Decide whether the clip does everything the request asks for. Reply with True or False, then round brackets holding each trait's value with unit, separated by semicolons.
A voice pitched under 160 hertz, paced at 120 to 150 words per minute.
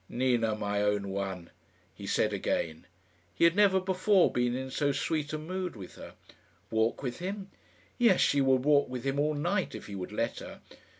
False (135 Hz; 190 wpm)